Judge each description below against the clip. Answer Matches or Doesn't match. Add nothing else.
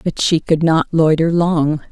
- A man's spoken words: Doesn't match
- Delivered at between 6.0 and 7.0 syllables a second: Doesn't match